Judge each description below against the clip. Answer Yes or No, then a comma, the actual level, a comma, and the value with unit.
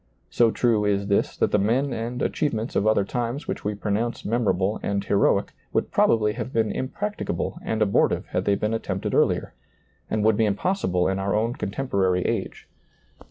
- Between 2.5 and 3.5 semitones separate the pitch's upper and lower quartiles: Yes, average, 2.9 semitones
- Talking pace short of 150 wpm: No, average, 180 wpm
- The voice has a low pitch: Yes, low, 110 Hz